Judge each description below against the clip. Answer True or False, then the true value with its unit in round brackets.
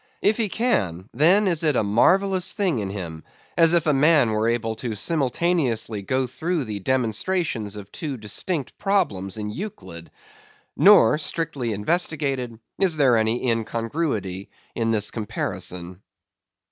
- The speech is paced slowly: False (145 wpm)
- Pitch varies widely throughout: True (7.7 semitones)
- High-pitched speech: False (120 Hz)